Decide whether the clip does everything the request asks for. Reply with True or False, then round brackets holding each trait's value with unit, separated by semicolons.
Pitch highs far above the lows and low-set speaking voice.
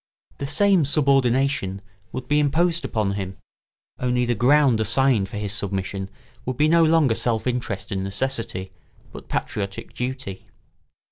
True (5.7 semitones; 125 Hz)